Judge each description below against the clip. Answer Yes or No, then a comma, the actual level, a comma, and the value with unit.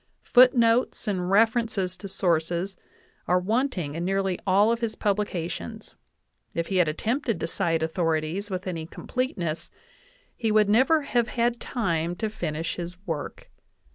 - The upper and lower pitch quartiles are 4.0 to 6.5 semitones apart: Yes, average, 5.1 semitones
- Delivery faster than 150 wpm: No, average, 145 wpm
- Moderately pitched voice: No, high, 195 Hz